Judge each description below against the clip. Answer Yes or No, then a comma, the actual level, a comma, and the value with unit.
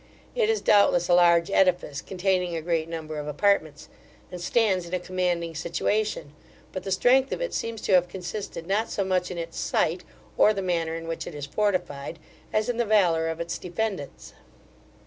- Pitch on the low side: No, medium, 180 Hz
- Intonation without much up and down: No, average, 3.4 semitones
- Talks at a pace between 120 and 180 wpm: No, average, 190 wpm